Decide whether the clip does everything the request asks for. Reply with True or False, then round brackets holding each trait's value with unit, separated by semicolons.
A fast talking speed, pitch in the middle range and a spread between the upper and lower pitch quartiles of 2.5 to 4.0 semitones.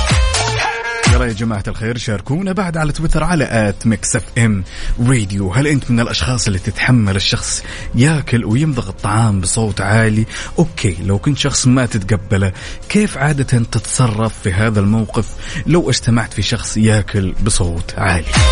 False (140 wpm; 110 Hz; 3.6 semitones)